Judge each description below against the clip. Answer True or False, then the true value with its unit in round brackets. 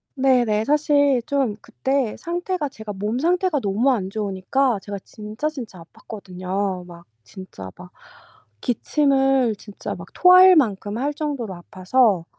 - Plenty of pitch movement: True (6.2 semitones)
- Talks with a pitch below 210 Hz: False (230 Hz)